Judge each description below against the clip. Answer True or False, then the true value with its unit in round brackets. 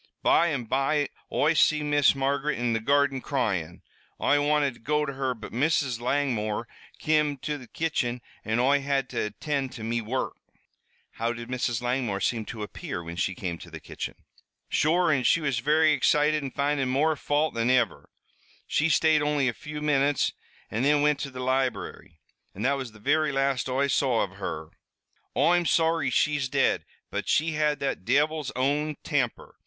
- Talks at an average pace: True (180 wpm)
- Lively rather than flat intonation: False (3.9 semitones)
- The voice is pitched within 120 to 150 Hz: True (135 Hz)